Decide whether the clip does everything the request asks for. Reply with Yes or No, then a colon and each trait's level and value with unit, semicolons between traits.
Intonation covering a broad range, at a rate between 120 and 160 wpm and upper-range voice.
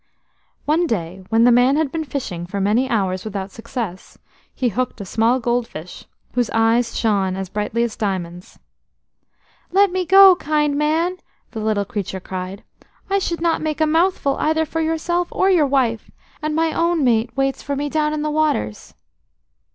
No: wide, 7.0 semitones; average, 175 wpm; very high, 250 Hz